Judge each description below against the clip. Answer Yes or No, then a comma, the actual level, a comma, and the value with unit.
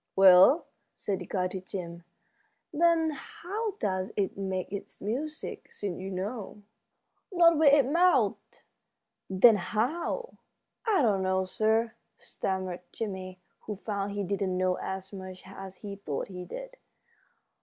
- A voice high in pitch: Yes, high, 200 Hz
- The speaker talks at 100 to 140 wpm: Yes, slow, 135 wpm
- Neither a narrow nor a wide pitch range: No, wide, 6.9 semitones